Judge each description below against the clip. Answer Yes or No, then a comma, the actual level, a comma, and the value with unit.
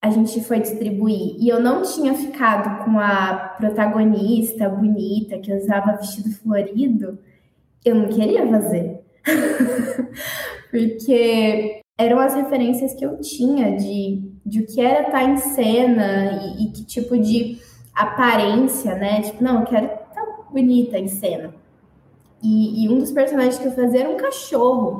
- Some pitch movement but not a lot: Yes, average, 3.3 semitones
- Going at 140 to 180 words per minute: Yes, average, 145 wpm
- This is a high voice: Yes, high, 225 Hz